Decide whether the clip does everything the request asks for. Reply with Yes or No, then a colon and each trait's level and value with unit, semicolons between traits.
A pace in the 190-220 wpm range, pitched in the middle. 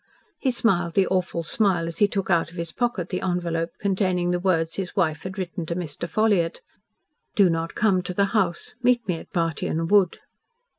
Yes: average, 195 wpm; medium, 180 Hz